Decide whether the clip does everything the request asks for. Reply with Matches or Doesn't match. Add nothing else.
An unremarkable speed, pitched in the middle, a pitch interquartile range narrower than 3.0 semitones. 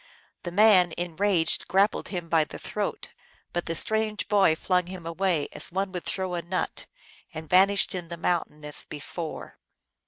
Matches